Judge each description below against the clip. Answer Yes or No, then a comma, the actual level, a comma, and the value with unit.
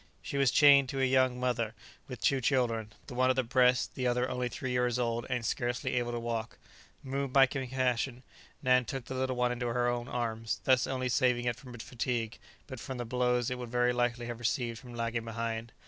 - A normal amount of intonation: No, narrow, 1.4 semitones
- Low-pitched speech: Yes, low, 125 Hz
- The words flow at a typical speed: No, fast, 220 wpm